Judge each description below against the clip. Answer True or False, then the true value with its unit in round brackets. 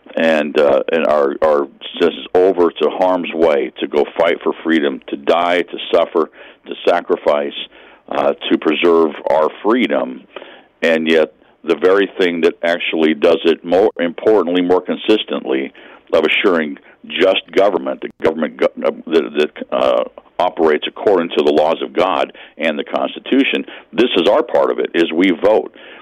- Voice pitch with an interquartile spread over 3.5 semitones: False (3.0 semitones)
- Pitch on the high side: False (85 Hz)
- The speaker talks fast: False (150 wpm)